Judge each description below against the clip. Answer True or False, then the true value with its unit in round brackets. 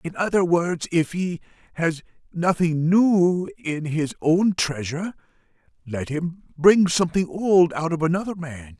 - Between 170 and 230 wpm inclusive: False (145 wpm)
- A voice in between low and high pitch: True (170 Hz)